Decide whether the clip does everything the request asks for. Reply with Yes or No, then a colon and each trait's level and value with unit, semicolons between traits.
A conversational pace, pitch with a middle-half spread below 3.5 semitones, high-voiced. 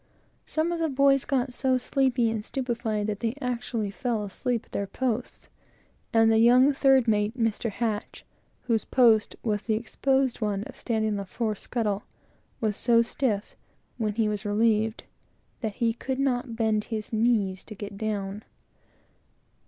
Yes: average, 155 wpm; average, 2.9 semitones; high, 225 Hz